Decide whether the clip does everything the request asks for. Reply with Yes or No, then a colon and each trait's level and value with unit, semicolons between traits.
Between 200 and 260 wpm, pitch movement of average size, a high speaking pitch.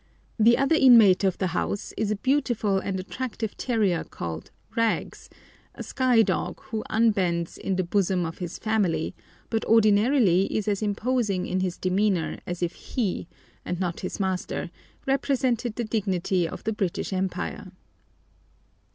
No: average, 150 wpm; average, 3.8 semitones; high, 200 Hz